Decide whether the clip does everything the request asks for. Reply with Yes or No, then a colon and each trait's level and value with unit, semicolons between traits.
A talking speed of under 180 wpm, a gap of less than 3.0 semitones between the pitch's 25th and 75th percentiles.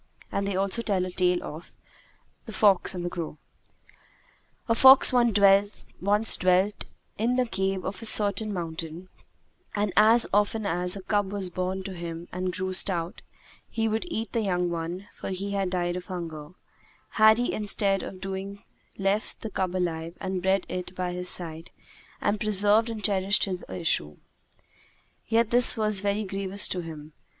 Yes: average, 170 wpm; narrow, 2.5 semitones